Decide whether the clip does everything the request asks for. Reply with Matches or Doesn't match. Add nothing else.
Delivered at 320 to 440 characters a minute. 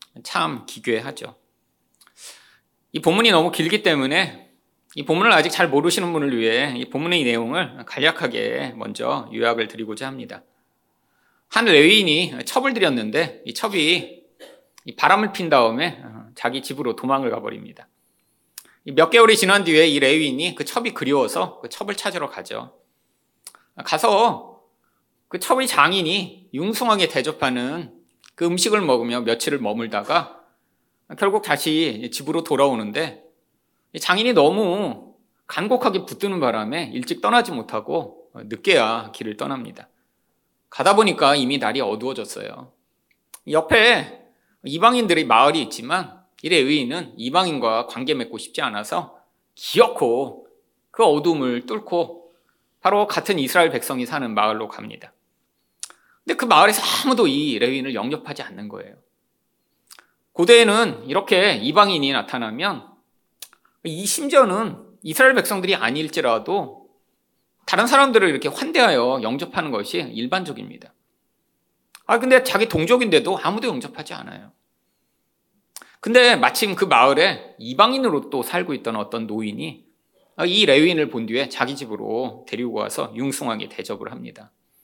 Doesn't match